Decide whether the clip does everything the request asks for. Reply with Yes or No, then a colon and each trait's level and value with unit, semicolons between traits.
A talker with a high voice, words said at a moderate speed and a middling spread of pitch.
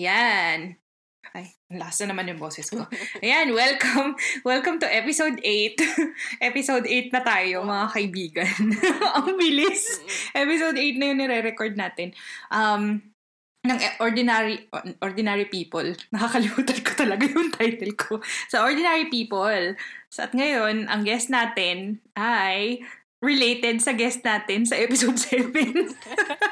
Yes: high, 235 Hz; average, 130 wpm; average, 4.9 semitones